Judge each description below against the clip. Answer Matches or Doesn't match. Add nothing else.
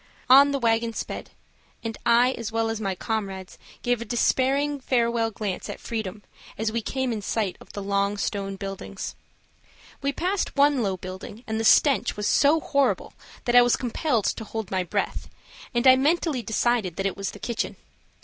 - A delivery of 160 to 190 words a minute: Matches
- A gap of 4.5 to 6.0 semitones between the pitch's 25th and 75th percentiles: Doesn't match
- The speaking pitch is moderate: Doesn't match